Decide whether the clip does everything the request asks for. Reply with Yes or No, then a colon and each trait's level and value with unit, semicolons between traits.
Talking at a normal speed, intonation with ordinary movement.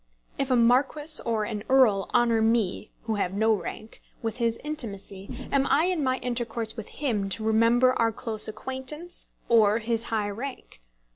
Yes: average, 165 wpm; average, 3.1 semitones